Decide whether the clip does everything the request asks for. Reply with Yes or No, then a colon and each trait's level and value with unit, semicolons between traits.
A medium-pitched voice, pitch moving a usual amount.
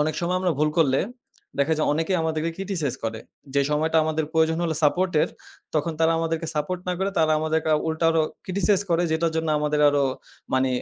No: medium, 160 Hz; narrow, 1.9 semitones